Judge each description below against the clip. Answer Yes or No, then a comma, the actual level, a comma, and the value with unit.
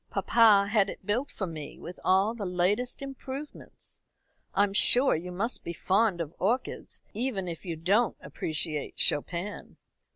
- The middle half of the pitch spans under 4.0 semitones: No, average, 4.8 semitones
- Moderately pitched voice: No, high, 195 Hz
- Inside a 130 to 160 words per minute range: Yes, average, 150 wpm